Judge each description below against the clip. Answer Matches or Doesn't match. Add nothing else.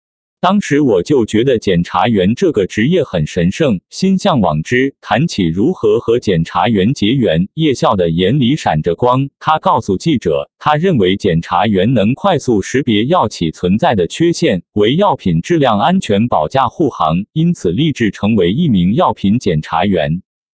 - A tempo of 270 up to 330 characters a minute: Doesn't match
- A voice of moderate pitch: Matches